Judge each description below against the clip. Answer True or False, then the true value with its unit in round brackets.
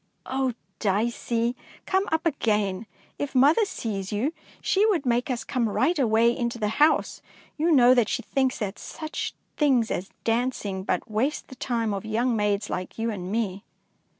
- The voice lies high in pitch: True (235 Hz)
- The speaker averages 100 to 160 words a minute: False (170 wpm)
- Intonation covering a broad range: False (4.1 semitones)